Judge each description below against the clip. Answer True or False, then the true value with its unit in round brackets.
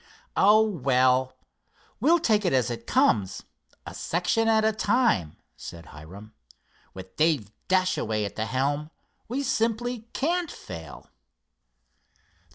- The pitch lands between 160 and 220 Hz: False (150 Hz)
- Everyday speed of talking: False (120 wpm)